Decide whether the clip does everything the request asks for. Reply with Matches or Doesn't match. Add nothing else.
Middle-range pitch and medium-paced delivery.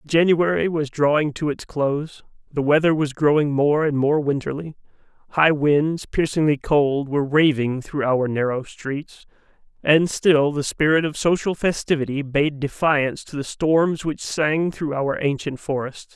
Matches